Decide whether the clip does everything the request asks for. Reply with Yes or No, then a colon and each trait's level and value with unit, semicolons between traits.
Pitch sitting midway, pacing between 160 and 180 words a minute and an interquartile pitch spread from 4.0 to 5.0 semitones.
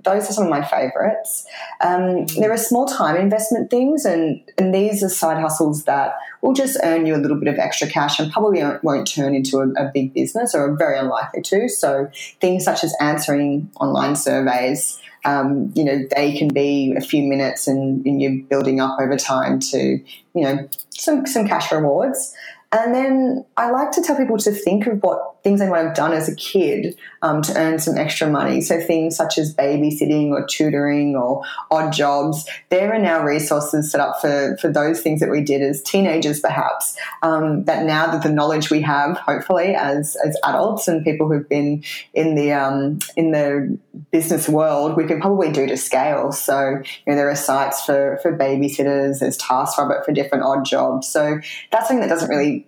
No: medium, 155 Hz; average, 200 wpm; average, 4.6 semitones